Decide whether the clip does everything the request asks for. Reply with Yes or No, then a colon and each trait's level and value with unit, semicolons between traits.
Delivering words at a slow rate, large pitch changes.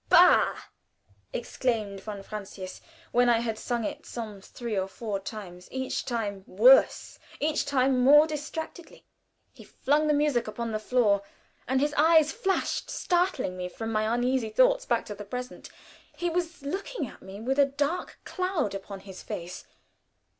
No: average, 160 wpm; wide, 6.1 semitones